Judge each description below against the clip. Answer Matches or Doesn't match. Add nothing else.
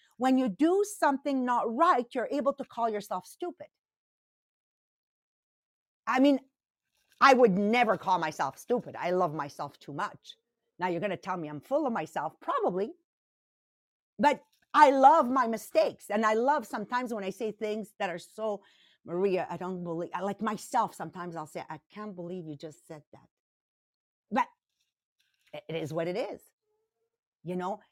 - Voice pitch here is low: Doesn't match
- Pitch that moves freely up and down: Matches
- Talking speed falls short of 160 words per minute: Doesn't match